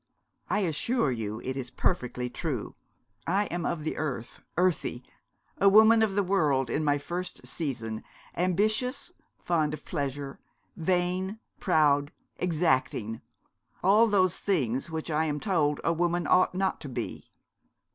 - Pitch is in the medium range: Yes, medium, 160 Hz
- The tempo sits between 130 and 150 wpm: Yes, average, 140 wpm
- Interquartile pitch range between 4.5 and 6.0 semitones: Yes, average, 5.1 semitones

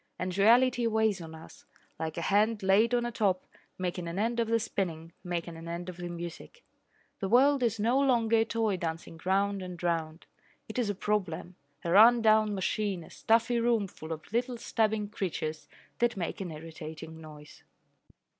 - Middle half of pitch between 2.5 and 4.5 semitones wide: No, average, 5.0 semitones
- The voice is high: Yes, high, 195 Hz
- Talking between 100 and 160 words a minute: No, average, 185 wpm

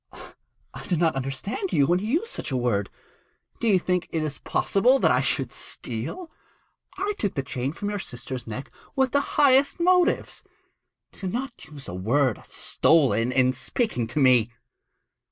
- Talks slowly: No, average, 170 wpm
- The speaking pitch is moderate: Yes, medium, 160 Hz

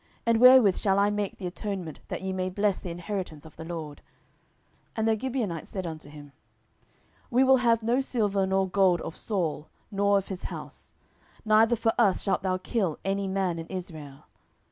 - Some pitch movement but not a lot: Yes, average, 3.8 semitones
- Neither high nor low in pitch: No, high, 195 Hz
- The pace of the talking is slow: No, average, 190 wpm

